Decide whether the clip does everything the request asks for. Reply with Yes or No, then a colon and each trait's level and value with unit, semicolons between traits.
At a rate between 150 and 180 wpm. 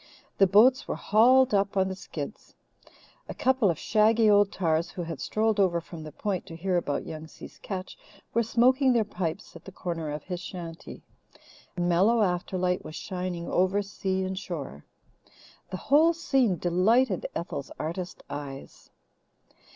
Yes: average, 160 wpm